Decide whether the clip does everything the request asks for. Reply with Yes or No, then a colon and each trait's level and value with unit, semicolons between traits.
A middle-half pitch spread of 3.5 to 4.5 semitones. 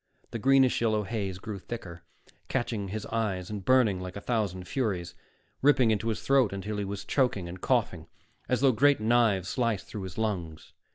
Yes: average, 4.0 semitones